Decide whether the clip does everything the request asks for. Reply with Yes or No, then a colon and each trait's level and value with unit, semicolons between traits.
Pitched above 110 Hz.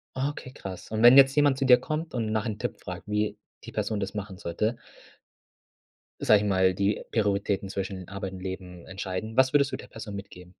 No: low, 105 Hz